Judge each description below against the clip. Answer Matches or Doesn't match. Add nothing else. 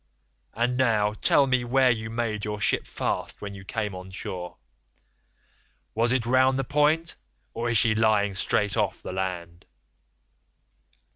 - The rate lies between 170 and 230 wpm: Doesn't match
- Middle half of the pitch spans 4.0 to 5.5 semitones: Doesn't match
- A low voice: Matches